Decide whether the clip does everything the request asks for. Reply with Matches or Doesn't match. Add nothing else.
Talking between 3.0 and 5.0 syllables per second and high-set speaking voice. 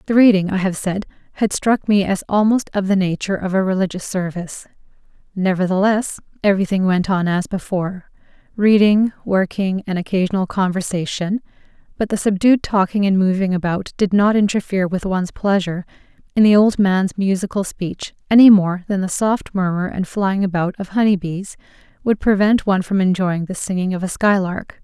Doesn't match